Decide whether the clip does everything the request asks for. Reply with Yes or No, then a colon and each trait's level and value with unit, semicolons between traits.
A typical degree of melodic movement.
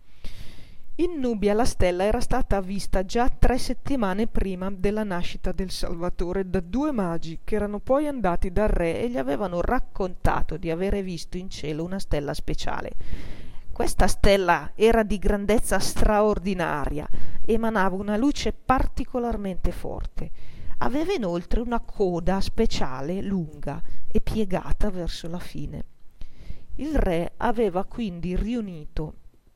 Yes: average, 4.0 semitones